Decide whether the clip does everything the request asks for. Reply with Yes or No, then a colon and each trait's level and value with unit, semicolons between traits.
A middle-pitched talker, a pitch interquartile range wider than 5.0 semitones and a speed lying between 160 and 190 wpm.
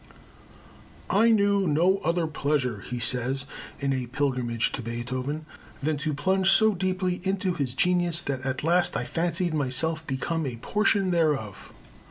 No: medium, 155 Hz; wide, 5.6 semitones; average, 150 wpm